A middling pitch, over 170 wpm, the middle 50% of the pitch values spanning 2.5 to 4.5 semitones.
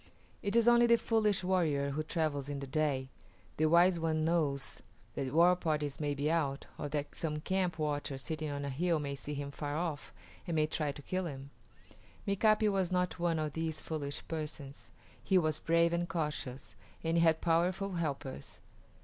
Yes: medium, 155 Hz; average, 185 wpm; average, 3.2 semitones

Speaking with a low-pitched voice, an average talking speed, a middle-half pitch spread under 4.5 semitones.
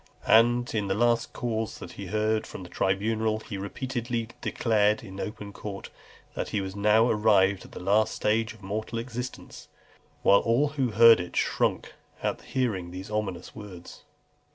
Yes: low, 110 Hz; average, 160 wpm; narrow, 2.5 semitones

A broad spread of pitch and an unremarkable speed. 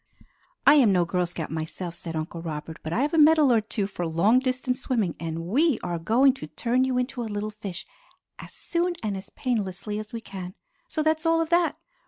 No: wide, 7.1 semitones; fast, 220 wpm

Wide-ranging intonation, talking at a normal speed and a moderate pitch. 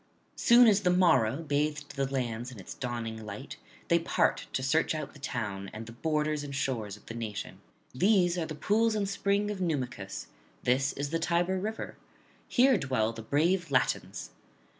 Yes: wide, 7.2 semitones; average, 180 wpm; medium, 145 Hz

